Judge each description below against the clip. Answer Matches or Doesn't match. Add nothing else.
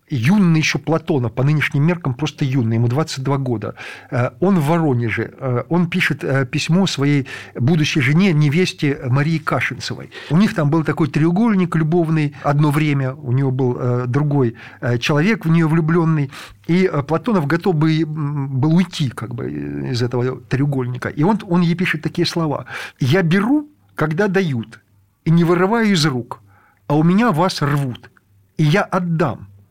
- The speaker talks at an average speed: Matches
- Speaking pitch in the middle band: Matches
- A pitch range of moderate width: Matches